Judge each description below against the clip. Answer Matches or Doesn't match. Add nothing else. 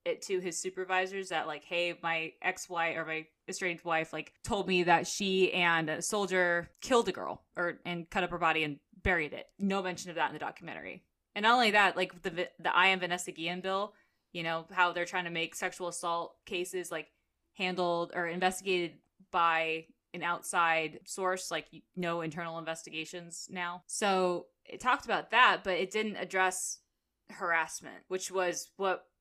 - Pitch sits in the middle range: Matches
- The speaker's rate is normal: Matches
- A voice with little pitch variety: Matches